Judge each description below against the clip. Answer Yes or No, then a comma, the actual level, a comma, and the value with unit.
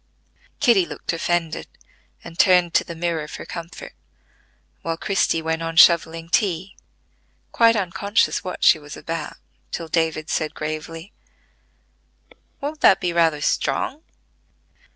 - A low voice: No, medium, 165 Hz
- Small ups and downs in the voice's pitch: Yes, narrow, 2.2 semitones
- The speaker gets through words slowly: Yes, slow, 125 wpm